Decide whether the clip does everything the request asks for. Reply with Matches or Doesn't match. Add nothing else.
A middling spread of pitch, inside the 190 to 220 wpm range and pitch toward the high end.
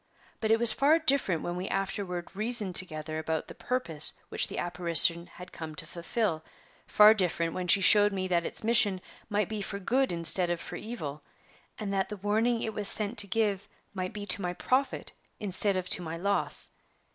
Matches